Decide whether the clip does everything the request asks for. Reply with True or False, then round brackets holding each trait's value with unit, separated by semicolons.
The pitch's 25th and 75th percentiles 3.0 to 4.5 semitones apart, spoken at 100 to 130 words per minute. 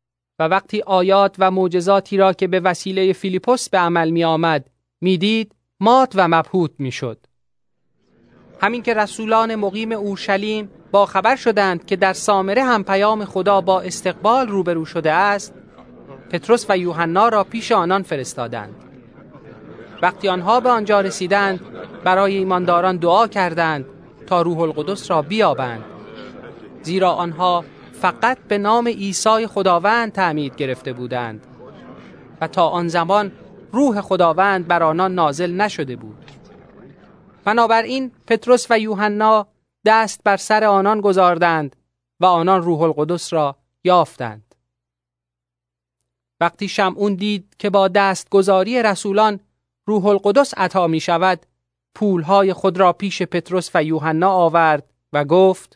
True (3.8 semitones; 125 wpm)